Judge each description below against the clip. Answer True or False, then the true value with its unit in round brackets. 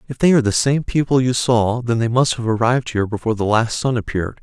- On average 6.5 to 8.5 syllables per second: True (6.6 syllables/s)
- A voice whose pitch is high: False (120 Hz)